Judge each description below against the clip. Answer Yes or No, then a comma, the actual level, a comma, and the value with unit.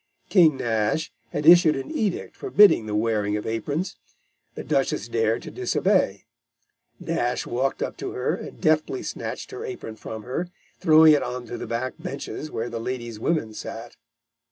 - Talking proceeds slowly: No, average, 165 wpm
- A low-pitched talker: Yes, low, 130 Hz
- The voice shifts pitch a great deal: Yes, wide, 6.8 semitones